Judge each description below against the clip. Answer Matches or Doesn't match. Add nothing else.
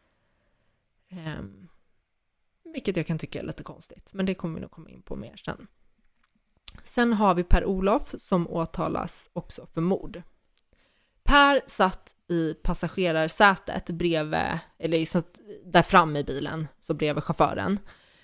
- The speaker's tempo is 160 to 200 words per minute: Doesn't match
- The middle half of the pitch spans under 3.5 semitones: Matches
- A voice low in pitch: Doesn't match